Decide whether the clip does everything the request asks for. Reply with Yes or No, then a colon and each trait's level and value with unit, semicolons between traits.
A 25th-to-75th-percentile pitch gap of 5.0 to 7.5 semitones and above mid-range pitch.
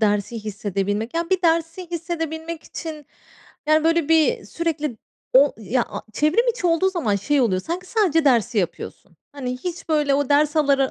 Yes: average, 5.3 semitones; very high, 300 Hz